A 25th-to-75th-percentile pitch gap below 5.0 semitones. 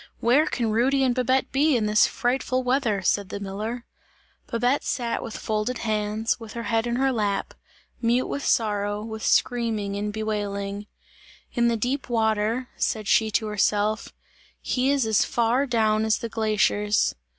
Yes: narrow, 2.6 semitones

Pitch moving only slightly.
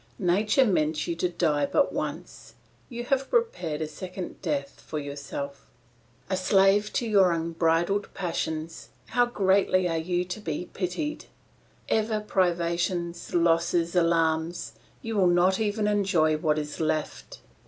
No: average, 3.6 semitones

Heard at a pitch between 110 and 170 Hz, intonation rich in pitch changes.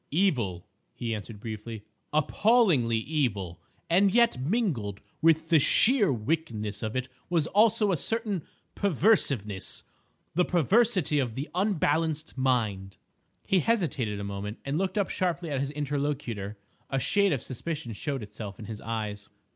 Yes: medium, 140 Hz; wide, 8.4 semitones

